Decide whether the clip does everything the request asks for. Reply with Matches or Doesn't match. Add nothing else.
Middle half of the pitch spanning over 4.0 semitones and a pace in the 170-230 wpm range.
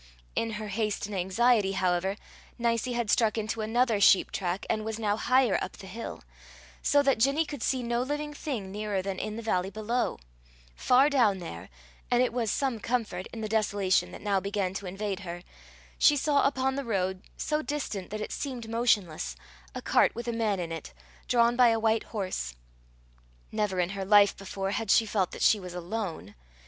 Doesn't match